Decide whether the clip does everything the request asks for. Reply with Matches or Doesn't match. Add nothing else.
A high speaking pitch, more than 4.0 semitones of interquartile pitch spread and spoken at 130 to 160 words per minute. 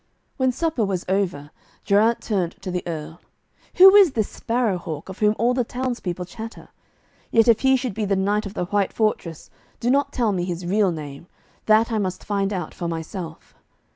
Doesn't match